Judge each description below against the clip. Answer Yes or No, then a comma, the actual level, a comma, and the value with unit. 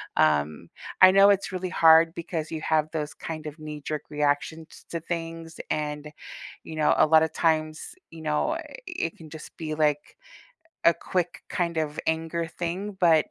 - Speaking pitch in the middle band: Yes, medium, 160 Hz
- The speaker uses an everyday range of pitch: No, narrow, 1.7 semitones